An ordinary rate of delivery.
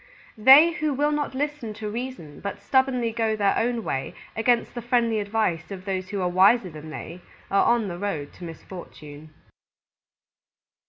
Yes: average, 165 wpm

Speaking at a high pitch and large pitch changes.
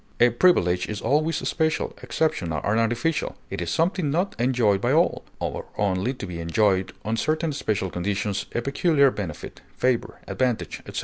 No: low, 120 Hz; wide, 7.5 semitones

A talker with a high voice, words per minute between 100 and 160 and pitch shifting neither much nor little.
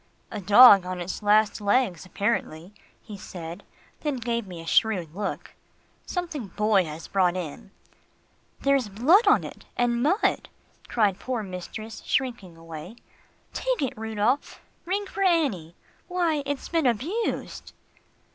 No: high, 215 Hz; slow, 135 wpm; wide, 6.6 semitones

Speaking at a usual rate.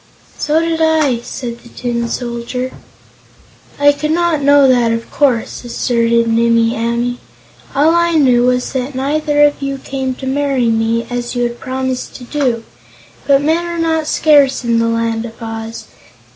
Yes: average, 165 wpm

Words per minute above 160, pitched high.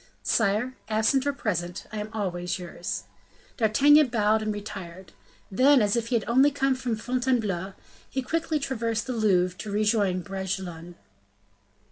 No: average, 145 wpm; high, 215 Hz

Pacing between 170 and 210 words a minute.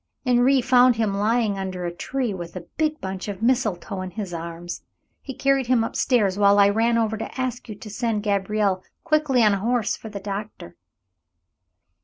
Yes: average, 190 wpm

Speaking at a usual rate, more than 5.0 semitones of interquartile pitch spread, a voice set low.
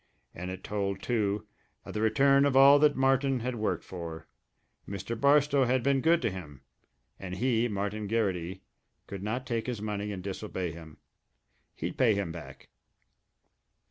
Yes: average, 160 wpm; wide, 5.4 semitones; low, 105 Hz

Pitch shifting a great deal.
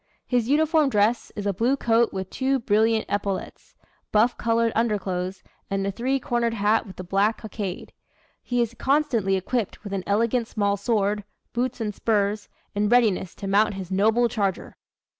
No: average, 3.0 semitones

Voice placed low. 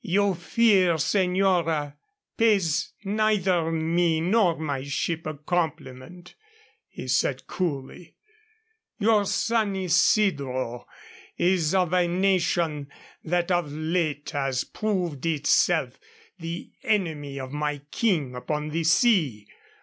No: medium, 170 Hz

